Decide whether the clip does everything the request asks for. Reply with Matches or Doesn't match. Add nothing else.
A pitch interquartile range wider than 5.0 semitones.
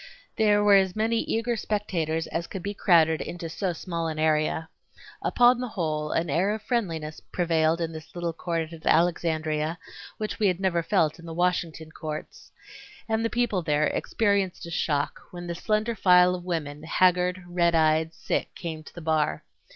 Doesn't match